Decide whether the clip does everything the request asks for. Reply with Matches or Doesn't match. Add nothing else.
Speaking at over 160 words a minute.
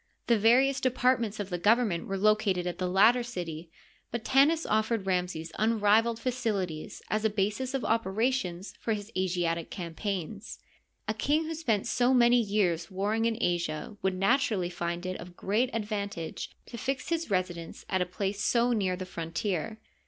Matches